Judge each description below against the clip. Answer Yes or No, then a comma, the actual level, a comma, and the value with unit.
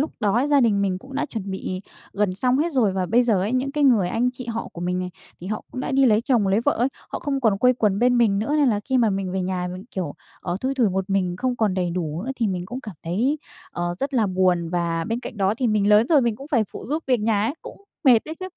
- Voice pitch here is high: Yes, high, 215 Hz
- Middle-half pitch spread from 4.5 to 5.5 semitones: Yes, average, 5.2 semitones